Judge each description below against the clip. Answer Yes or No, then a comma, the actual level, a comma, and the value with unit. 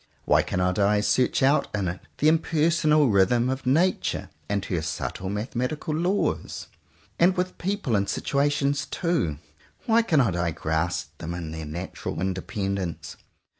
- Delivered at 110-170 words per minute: Yes, average, 140 wpm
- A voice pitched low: Yes, low, 110 Hz